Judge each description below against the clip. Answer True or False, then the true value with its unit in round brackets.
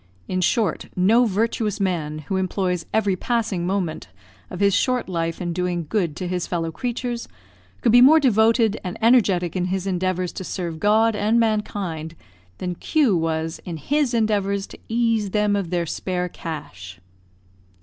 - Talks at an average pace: True (160 wpm)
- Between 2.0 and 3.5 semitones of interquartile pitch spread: False (4.1 semitones)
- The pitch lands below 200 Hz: True (190 Hz)